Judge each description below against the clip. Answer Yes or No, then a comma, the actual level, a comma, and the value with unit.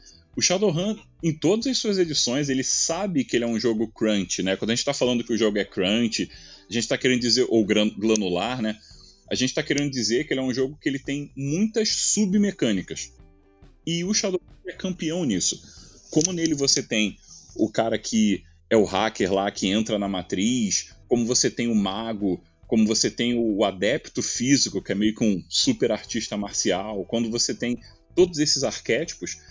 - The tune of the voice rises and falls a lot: Yes, wide, 6.2 semitones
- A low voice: Yes, low, 115 Hz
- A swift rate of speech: Yes, fast, 195 wpm